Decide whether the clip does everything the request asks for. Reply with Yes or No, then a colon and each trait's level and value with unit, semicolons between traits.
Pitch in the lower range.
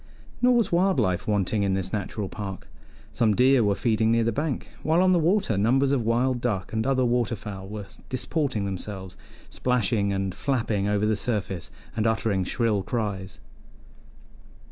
Yes: low, 110 Hz